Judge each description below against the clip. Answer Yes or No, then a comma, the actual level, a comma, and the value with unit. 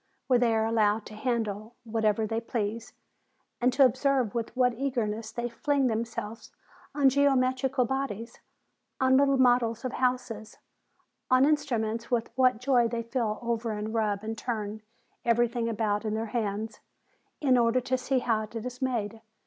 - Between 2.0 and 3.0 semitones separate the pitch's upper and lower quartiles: Yes, narrow, 2.5 semitones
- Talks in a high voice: Yes, high, 235 Hz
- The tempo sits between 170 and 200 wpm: No, average, 155 wpm